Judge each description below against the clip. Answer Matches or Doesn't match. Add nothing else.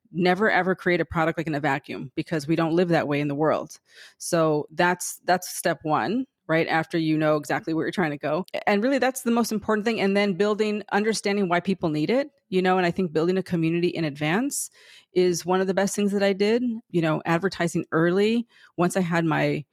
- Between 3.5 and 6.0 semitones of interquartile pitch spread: Matches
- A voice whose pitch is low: Doesn't match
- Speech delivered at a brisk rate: Matches